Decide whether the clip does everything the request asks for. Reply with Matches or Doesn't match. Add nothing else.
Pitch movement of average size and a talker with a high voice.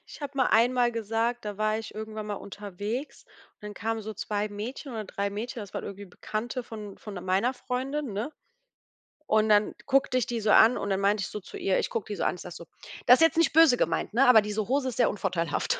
Matches